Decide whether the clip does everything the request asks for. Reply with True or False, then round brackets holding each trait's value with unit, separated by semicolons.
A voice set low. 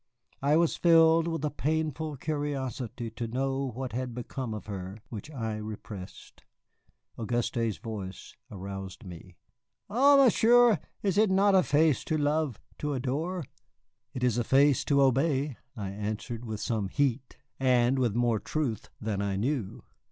True (130 Hz)